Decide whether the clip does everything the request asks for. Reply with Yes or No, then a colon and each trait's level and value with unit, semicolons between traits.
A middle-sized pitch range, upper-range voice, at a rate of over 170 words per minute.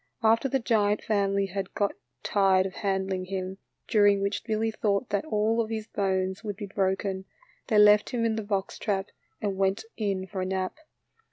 No: narrow, 2.1 semitones; high, 200 Hz; average, 185 wpm